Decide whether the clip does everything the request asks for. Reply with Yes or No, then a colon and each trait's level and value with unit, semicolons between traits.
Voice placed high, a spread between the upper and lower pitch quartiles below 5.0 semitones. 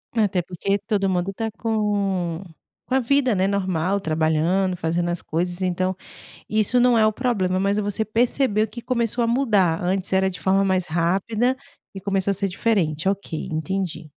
Yes: high, 195 Hz; average, 3.4 semitones